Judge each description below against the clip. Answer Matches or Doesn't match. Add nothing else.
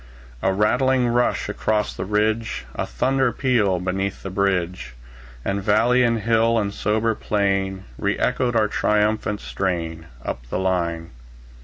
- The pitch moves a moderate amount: Matches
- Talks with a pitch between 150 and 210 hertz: Doesn't match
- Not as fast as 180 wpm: Matches